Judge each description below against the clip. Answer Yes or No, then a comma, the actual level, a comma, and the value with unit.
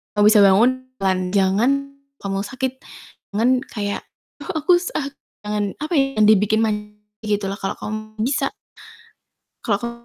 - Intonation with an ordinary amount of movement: Yes, average, 4.1 semitones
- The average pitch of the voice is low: No, high, 215 Hz